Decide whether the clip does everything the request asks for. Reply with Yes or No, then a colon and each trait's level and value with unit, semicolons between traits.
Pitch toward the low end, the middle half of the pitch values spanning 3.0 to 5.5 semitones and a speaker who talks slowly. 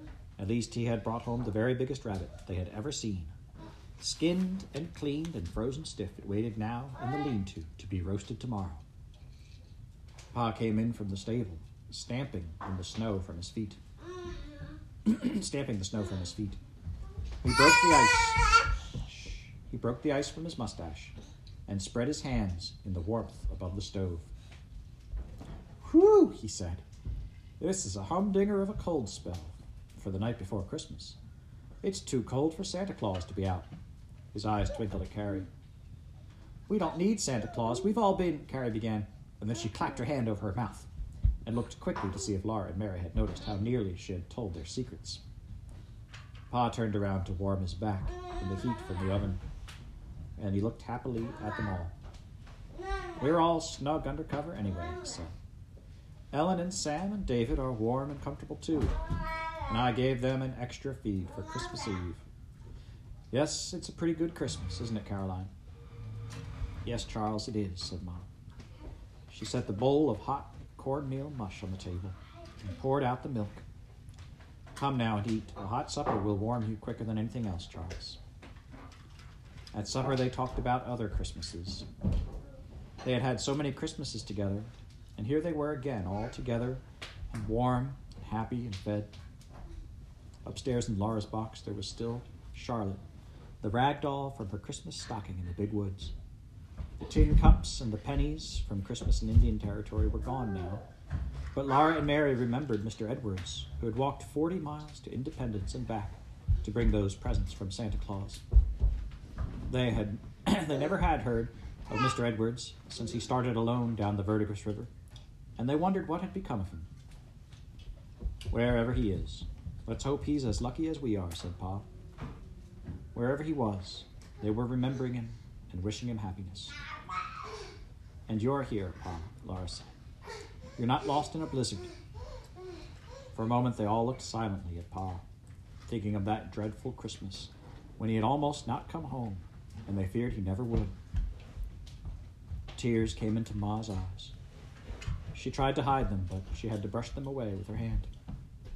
No: low, 110 Hz; average, 4.3 semitones; average, 170 wpm